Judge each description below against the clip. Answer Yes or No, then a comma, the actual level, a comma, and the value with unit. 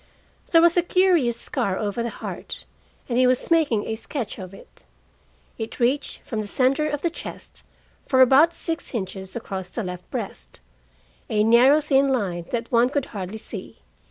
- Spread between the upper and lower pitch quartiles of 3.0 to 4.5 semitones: No, wide, 5.6 semitones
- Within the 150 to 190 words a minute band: Yes, average, 175 wpm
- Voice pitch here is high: Yes, high, 240 Hz